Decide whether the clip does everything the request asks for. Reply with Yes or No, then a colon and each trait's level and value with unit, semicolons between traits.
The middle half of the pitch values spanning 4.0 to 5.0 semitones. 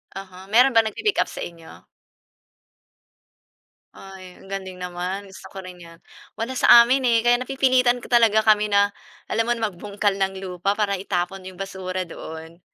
No: average, 3.6 semitones